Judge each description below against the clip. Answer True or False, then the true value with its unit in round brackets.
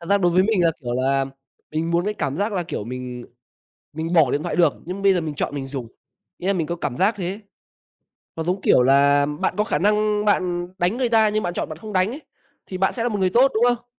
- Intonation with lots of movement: True (5.8 semitones)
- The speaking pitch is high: False (180 Hz)